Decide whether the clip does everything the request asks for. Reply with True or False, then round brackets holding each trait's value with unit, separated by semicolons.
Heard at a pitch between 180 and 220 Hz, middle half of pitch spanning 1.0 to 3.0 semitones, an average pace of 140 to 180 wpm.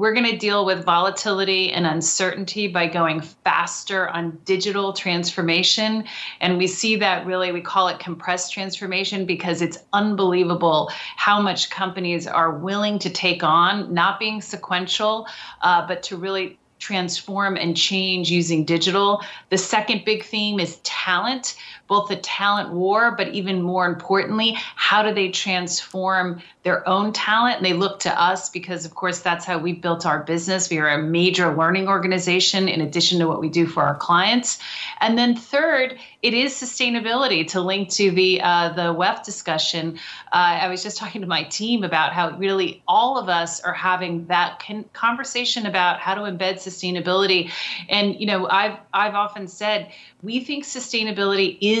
True (190 Hz; 2.7 semitones; 170 wpm)